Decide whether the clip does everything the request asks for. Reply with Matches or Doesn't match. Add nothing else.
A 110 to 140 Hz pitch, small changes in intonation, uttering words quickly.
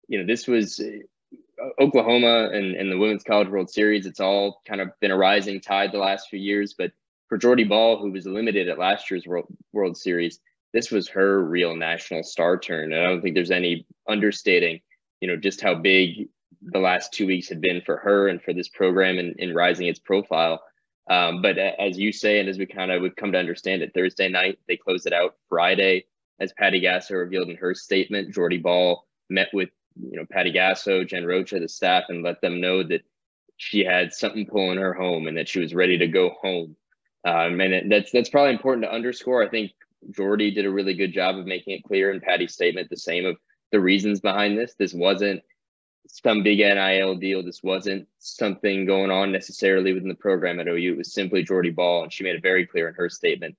Doesn't match